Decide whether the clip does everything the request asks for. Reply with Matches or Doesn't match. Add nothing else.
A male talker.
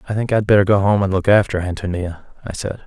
Matches